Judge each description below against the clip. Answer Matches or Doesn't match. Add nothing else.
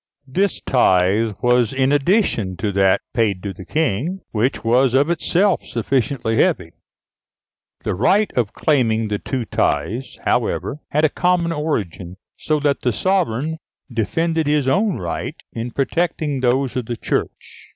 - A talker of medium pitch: Doesn't match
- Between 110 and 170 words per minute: Matches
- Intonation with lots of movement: Matches